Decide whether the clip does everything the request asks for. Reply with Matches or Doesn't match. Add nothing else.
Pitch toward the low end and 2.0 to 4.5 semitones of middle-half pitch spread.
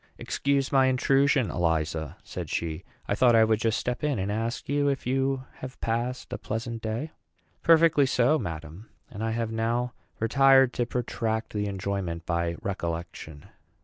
Doesn't match